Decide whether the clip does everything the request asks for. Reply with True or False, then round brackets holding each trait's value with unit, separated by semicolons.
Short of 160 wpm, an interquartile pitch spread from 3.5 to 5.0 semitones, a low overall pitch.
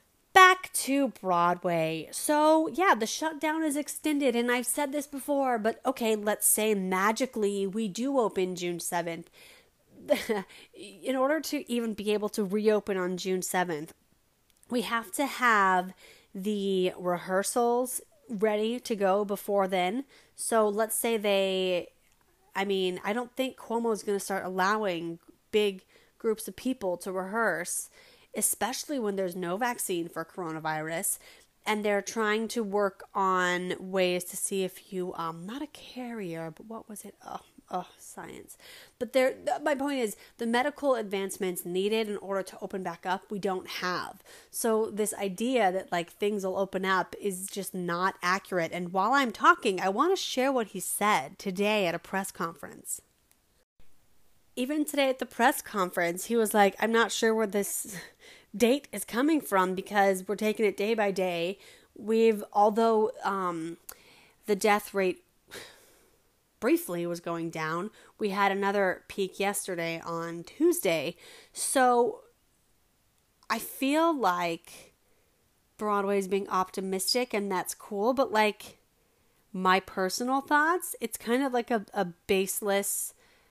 False (150 wpm; 4.7 semitones; 205 Hz)